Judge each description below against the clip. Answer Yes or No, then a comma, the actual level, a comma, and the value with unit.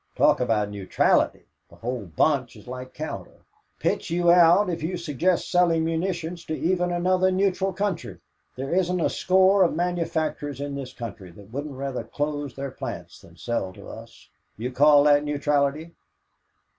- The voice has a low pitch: No, medium, 155 Hz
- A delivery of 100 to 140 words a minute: No, average, 165 wpm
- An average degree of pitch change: Yes, average, 4.9 semitones